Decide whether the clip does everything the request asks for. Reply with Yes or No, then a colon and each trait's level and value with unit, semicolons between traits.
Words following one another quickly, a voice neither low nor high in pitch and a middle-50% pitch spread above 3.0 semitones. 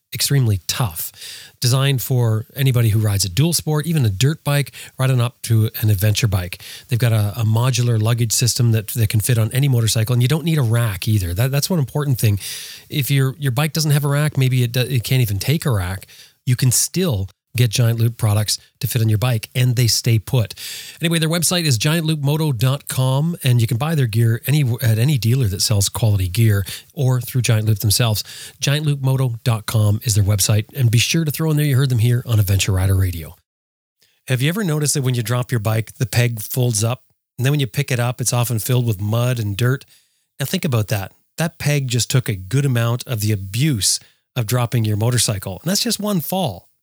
No: fast, 220 wpm; low, 125 Hz; average, 3.9 semitones